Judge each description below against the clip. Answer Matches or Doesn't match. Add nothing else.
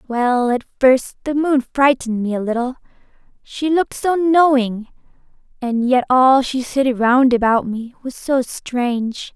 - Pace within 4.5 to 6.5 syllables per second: Doesn't match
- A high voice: Matches